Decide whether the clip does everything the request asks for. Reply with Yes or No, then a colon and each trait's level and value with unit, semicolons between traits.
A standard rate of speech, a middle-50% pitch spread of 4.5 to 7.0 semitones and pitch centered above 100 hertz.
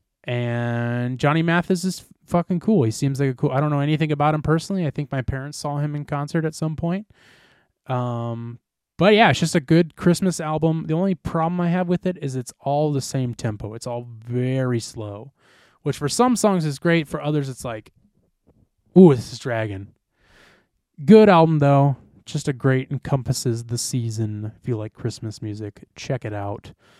Yes: average, 190 wpm; average, 5.2 semitones; medium, 140 Hz